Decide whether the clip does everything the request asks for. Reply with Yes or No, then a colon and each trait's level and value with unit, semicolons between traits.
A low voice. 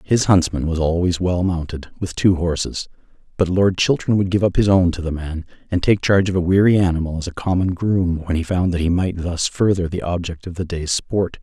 Yes: very low, 90 Hz